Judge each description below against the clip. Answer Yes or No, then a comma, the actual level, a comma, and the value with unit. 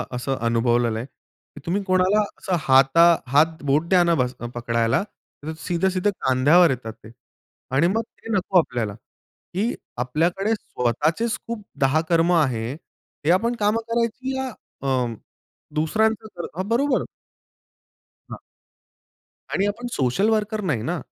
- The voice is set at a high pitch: No, medium, 170 Hz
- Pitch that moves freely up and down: Yes, wide, 8.0 semitones